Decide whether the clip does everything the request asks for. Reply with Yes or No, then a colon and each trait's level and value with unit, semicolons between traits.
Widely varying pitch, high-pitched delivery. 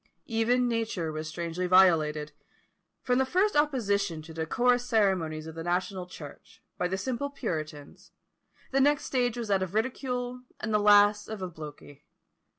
Yes: wide, 7.1 semitones; high, 200 Hz